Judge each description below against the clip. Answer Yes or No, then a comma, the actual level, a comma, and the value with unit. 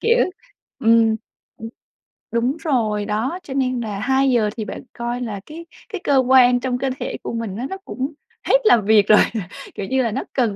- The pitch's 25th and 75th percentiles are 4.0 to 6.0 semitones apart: No, average, 3.3 semitones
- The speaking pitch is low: No, high, 245 Hz